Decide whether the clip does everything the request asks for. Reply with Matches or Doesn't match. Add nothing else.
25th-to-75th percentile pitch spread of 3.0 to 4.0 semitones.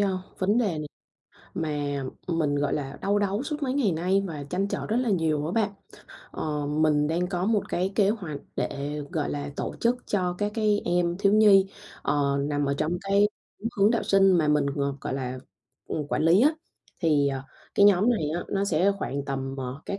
Doesn't match